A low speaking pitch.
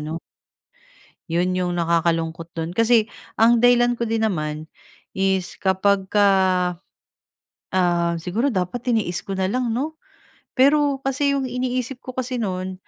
No: high, 200 Hz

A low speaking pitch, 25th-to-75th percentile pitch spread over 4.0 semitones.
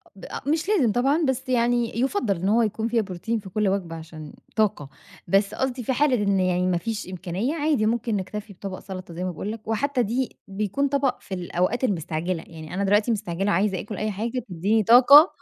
No: high, 210 Hz; average, 4.7 semitones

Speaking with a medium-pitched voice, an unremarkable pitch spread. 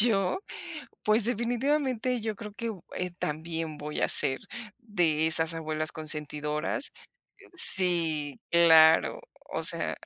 No: medium, 170 Hz; wide, 6.2 semitones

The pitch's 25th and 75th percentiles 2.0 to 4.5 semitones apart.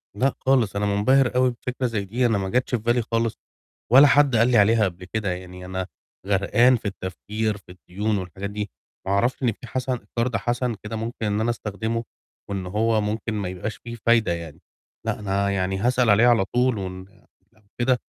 Yes: average, 3.4 semitones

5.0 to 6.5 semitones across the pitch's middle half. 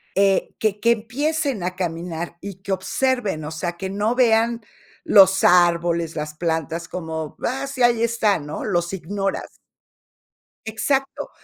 Yes: average, 5.3 semitones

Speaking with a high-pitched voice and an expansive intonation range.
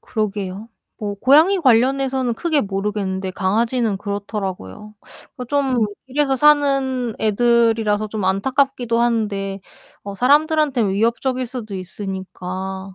No: high, 225 Hz; average, 4.9 semitones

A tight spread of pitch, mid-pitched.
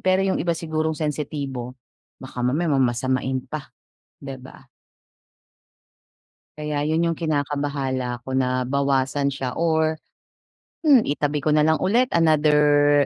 No: average, 3.0 semitones; medium, 145 Hz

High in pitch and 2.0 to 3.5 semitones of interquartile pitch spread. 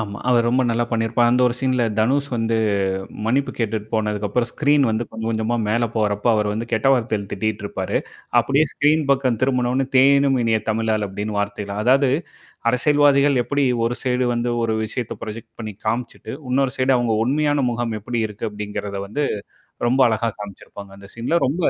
No: low, 115 Hz; average, 3.1 semitones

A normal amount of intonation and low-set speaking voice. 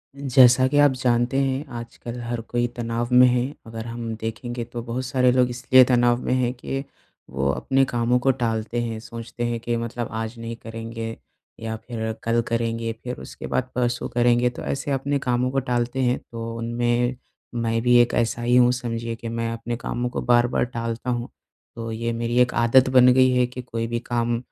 No: narrow, 1.3 semitones; low, 120 Hz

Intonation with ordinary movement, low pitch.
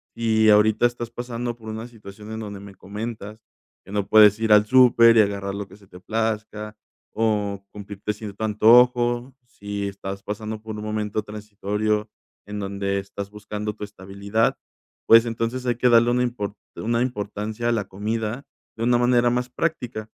No: narrow, 2.3 semitones; low, 110 Hz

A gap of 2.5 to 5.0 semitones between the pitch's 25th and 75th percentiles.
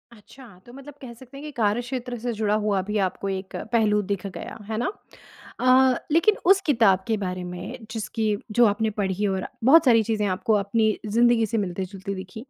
Yes: average, 3.5 semitones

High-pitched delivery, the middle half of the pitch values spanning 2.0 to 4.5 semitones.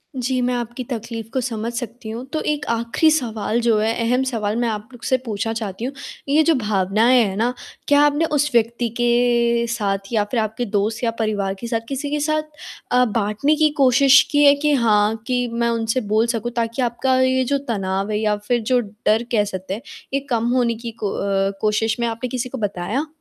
Yes: high, 235 Hz; average, 2.9 semitones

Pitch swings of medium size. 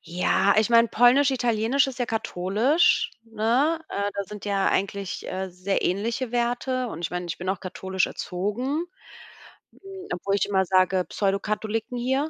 Yes: average, 4.3 semitones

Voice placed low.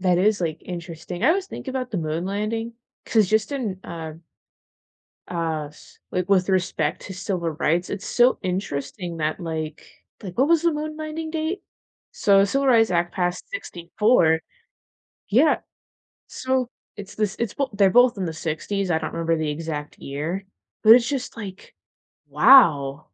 No: high, 190 Hz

